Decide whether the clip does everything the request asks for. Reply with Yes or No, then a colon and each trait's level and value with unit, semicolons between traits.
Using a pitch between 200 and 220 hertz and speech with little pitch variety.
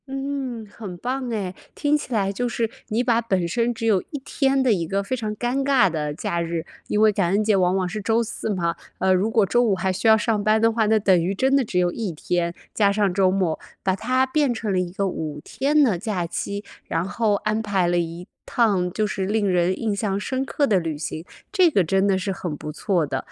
No: high, 205 Hz; average, 4.2 semitones